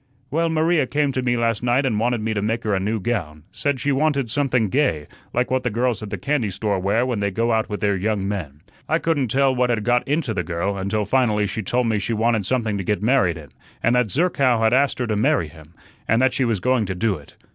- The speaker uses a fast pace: Yes, fast, 260 wpm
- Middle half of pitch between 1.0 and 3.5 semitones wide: No, average, 4.1 semitones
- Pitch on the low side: Yes, low, 115 Hz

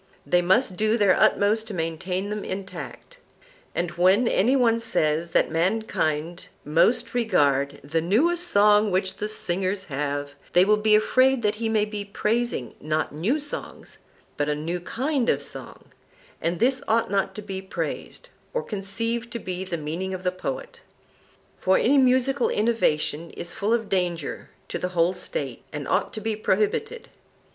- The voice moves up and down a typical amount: Yes, average, 5.0 semitones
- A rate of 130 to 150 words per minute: No, average, 165 wpm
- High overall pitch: Yes, high, 200 Hz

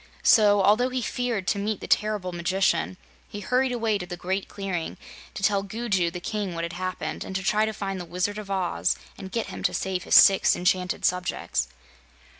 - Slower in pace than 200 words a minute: No, fast, 205 wpm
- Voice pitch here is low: No, high, 195 Hz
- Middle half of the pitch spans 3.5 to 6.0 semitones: No, average, 2.7 semitones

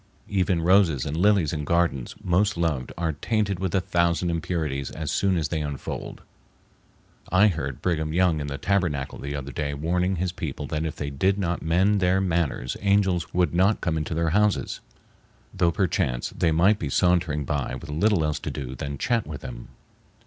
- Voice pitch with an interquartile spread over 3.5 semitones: Yes, average, 4.0 semitones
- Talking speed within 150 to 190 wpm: Yes, average, 185 wpm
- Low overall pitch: Yes, very low, 85 Hz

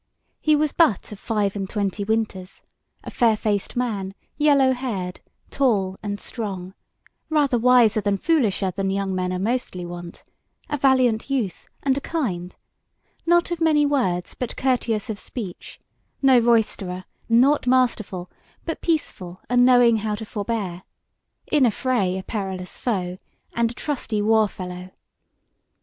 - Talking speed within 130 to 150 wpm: Yes, average, 145 wpm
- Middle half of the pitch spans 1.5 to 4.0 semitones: No, average, 5.1 semitones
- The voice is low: No, high, 220 Hz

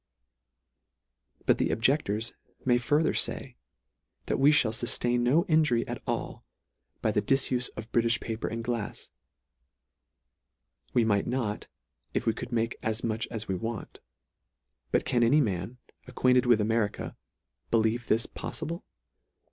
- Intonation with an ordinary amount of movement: No, narrow, 2.2 semitones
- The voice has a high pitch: No, low, 120 Hz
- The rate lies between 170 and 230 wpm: No, average, 140 wpm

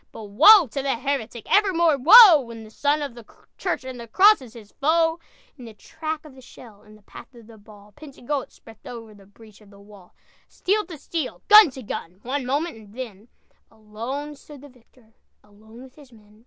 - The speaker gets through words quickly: Yes, fast, 210 wpm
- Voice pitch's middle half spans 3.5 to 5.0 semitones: No, wide, 5.4 semitones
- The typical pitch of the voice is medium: No, very high, 250 Hz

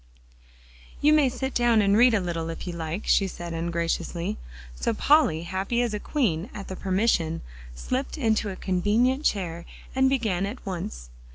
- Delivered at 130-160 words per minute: No, average, 170 wpm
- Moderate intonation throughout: No, wide, 5.9 semitones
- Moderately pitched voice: No, high, 195 Hz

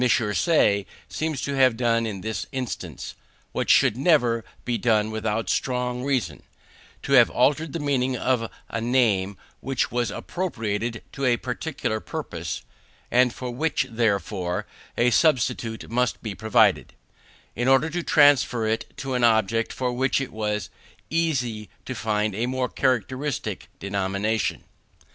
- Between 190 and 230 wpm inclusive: No, average, 140 wpm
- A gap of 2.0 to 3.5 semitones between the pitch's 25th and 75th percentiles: Yes, average, 3.2 semitones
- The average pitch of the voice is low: Yes, low, 120 Hz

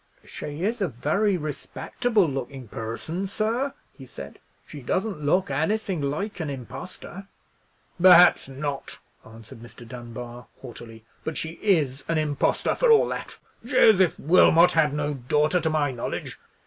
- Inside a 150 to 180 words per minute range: No, average, 140 wpm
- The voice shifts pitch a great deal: Yes, wide, 6.0 semitones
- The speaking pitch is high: No, medium, 150 Hz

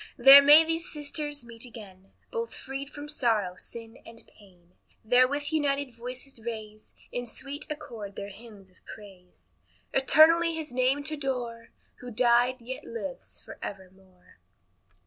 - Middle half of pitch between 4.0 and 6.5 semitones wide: Yes, average, 5.1 semitones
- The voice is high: Yes, high, 245 Hz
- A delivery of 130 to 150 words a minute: Yes, average, 140 wpm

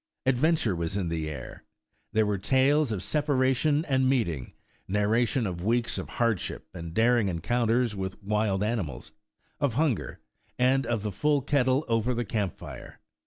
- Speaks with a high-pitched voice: No, low, 115 Hz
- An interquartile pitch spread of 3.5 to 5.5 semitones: Yes, average, 4.9 semitones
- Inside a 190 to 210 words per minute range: No, average, 165 wpm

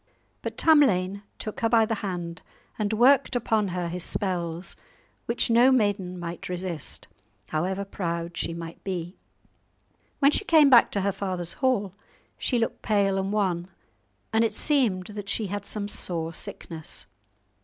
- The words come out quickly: No, average, 155 wpm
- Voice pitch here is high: Yes, high, 195 Hz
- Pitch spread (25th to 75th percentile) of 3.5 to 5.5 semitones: Yes, average, 4.1 semitones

